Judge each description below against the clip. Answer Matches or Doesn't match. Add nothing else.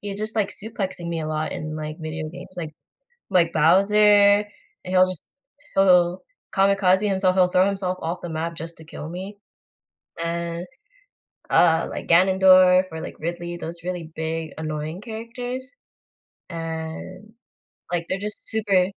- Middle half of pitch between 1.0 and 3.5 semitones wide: Matches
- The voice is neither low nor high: Matches